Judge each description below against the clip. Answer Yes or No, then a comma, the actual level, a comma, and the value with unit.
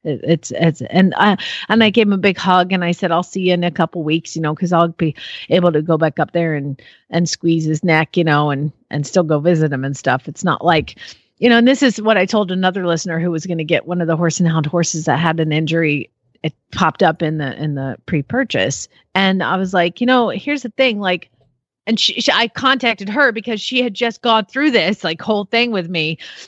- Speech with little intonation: No, average, 4.7 semitones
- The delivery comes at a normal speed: No, fast, 255 wpm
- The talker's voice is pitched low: No, medium, 175 Hz